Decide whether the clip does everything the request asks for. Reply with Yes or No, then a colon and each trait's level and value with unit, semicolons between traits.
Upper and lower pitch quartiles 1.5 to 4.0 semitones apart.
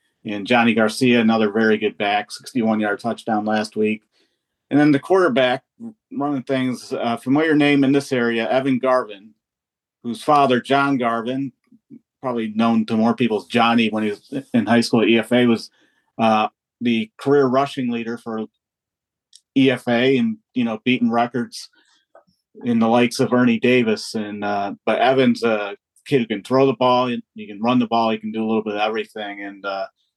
Yes: average, 3.2 semitones